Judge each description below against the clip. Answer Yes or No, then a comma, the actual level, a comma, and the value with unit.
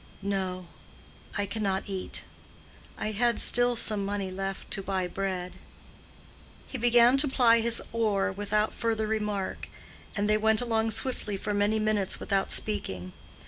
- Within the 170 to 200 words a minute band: No, average, 140 wpm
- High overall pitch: Yes, high, 210 Hz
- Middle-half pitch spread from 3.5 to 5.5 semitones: No, narrow, 2.5 semitones